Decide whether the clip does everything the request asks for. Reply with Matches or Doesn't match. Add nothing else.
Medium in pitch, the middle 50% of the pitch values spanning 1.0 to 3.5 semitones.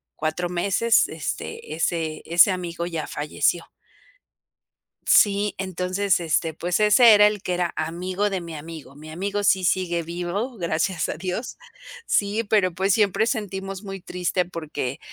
Matches